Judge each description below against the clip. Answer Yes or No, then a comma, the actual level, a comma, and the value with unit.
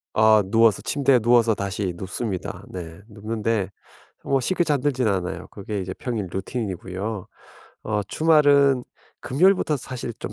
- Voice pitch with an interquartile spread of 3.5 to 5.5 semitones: Yes, average, 5.1 semitones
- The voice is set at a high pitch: No, low, 110 Hz